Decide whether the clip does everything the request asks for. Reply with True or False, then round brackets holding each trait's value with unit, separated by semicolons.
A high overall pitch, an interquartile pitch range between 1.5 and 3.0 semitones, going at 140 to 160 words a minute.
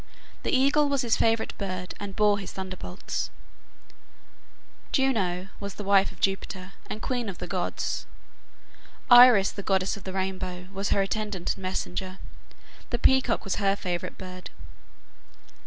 True (195 Hz; 2.7 semitones; 150 wpm)